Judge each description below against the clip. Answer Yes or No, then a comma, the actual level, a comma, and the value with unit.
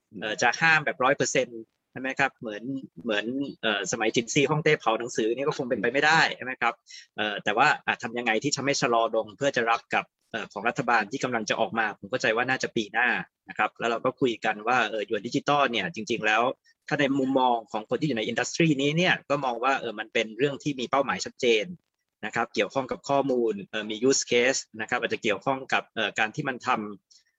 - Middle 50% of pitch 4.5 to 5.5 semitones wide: No, average, 3.6 semitones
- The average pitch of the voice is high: No, low, 135 Hz